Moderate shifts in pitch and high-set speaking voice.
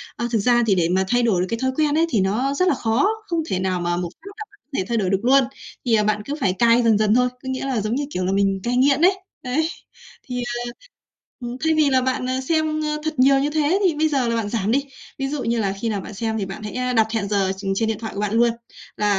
Yes: average, 4.7 semitones; high, 240 Hz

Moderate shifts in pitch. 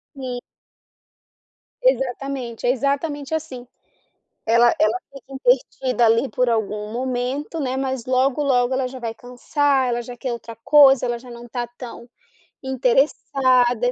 No: narrow, 2.2 semitones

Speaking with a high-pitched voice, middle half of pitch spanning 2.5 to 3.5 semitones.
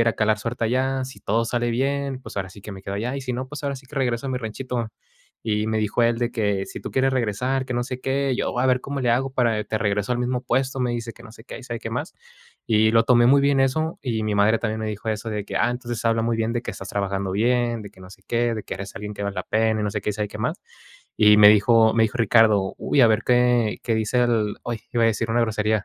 No: low, 115 Hz; average, 2.8 semitones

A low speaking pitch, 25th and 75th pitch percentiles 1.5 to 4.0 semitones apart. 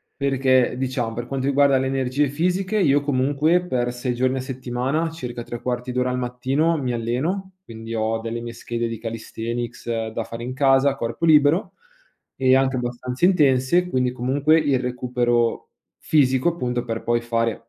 Yes: low, 130 Hz; average, 2.8 semitones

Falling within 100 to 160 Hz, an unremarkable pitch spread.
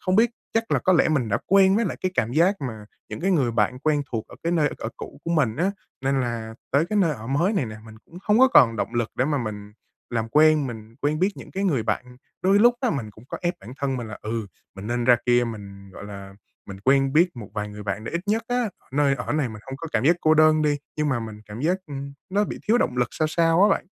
No: low, 135 Hz; wide, 7.0 semitones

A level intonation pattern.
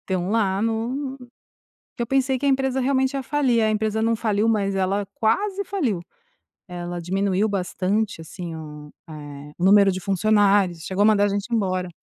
No: average, 3.9 semitones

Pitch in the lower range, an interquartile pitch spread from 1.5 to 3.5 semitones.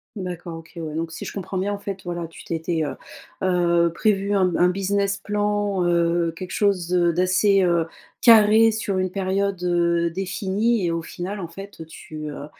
No: medium, 185 Hz; average, 2.8 semitones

